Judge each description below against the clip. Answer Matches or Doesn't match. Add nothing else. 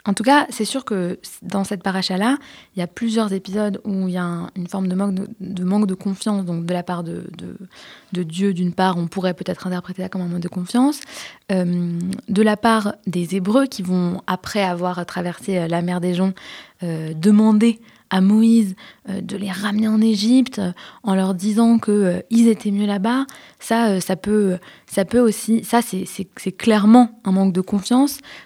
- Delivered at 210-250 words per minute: Doesn't match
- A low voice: Doesn't match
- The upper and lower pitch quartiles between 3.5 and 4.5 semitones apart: Doesn't match